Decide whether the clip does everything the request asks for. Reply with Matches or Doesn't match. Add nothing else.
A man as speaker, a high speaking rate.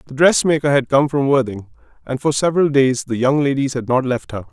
Matches